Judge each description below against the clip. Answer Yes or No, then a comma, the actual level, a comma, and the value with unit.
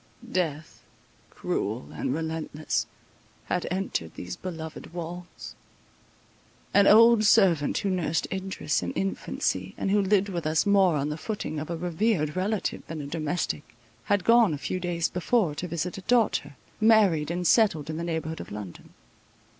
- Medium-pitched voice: Yes, medium, 170 Hz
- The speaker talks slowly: No, average, 160 wpm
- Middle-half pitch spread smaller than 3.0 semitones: No, average, 4.2 semitones